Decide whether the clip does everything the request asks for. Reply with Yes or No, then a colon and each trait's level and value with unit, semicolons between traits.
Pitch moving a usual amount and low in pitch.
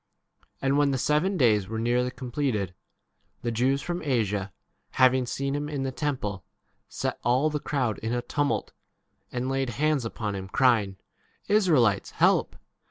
Yes: average, 4.2 semitones; low, 130 Hz